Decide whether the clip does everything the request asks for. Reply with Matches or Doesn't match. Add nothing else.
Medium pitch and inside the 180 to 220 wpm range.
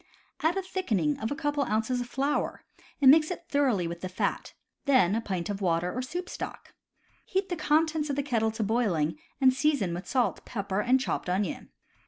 Doesn't match